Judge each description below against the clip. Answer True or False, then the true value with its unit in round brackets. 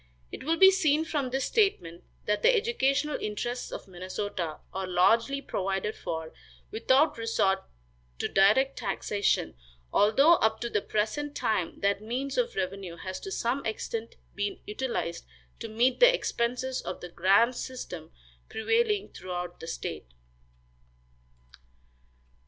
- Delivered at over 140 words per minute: False (135 wpm)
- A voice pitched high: True (225 Hz)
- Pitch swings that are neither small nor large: False (6.4 semitones)